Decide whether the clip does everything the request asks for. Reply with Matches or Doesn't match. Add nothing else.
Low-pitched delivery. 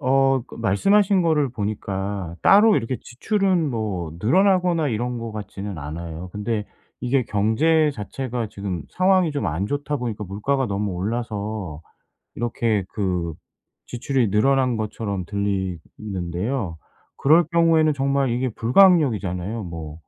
Matches